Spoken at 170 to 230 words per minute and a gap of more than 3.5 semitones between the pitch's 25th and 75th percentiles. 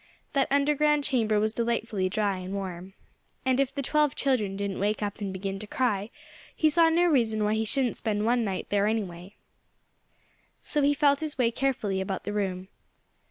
Yes: average, 185 wpm; wide, 5.6 semitones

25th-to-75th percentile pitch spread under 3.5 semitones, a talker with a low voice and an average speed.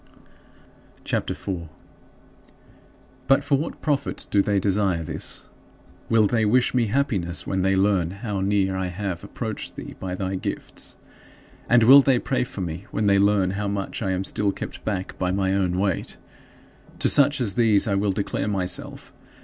Yes: average, 2.9 semitones; low, 100 Hz; average, 175 wpm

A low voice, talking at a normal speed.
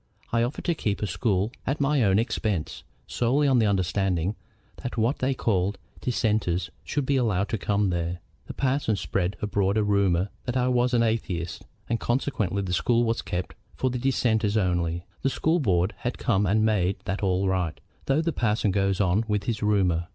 Yes: low, 105 Hz; average, 190 wpm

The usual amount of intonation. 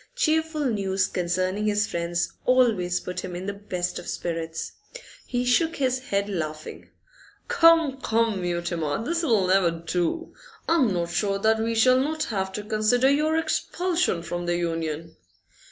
No: wide, 6.7 semitones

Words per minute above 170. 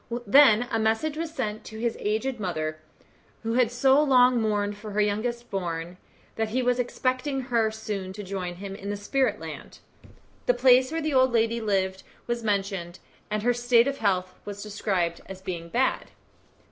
Yes: average, 180 wpm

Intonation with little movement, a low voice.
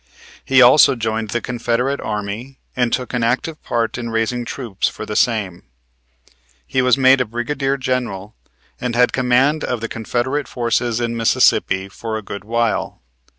Yes: narrow, 2.3 semitones; low, 120 Hz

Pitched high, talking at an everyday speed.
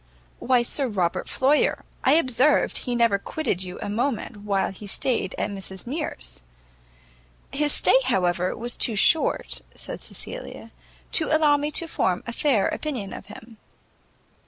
Yes: high, 235 Hz; average, 150 wpm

